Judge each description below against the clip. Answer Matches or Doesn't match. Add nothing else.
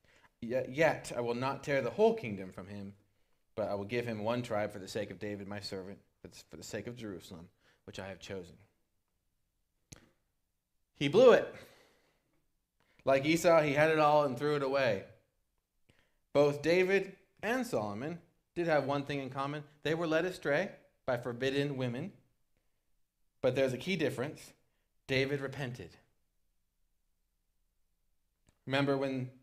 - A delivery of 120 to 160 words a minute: Matches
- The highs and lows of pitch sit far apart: Matches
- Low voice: Matches